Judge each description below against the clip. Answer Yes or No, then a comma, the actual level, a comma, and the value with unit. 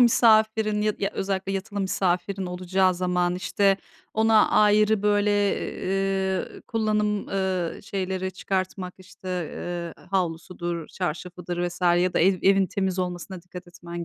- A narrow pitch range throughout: Yes, narrow, 2.0 semitones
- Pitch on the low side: No, high, 190 Hz